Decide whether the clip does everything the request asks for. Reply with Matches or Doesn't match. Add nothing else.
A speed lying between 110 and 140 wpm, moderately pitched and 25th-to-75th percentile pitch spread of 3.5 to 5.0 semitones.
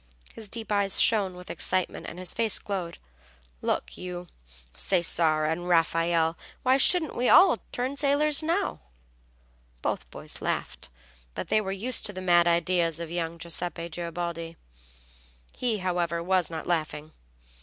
Matches